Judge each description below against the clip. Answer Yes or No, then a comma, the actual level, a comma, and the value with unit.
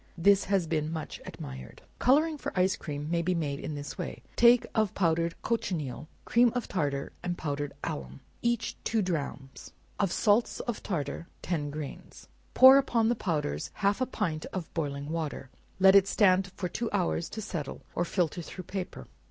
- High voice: No, medium, 175 Hz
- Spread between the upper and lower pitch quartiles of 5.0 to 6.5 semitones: Yes, wide, 5.5 semitones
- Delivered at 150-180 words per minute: Yes, average, 175 wpm